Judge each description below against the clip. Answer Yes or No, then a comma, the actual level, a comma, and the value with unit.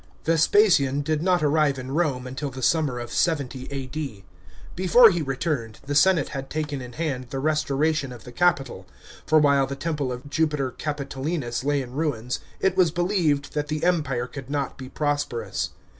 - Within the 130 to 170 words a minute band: No, average, 185 wpm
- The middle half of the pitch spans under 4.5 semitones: Yes, average, 3.2 semitones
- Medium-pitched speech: Yes, medium, 145 Hz